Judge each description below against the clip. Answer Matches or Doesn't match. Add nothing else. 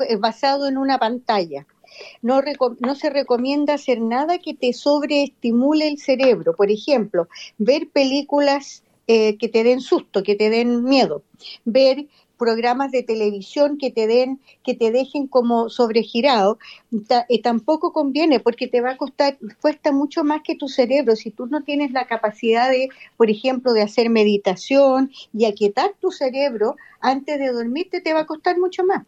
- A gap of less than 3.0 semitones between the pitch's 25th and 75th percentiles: Doesn't match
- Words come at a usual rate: Matches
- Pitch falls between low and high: Doesn't match